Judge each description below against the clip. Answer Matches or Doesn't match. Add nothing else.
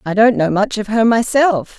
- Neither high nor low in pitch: Doesn't match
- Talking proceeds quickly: Matches